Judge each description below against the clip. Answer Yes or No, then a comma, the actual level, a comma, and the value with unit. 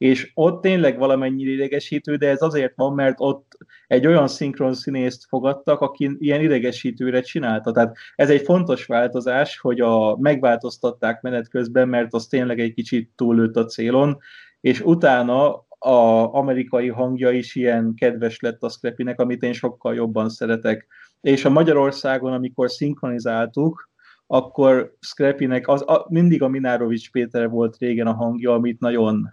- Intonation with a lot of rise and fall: No, narrow, 2.6 semitones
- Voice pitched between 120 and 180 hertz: Yes, low, 125 Hz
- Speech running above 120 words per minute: Yes, average, 150 wpm